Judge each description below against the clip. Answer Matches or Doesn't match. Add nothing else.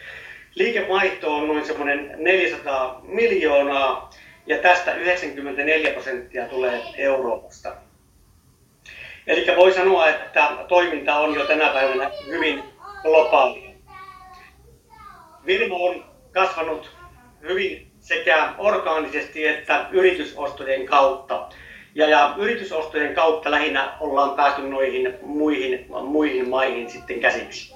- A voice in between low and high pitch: Matches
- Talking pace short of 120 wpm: Matches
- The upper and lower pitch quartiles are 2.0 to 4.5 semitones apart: Doesn't match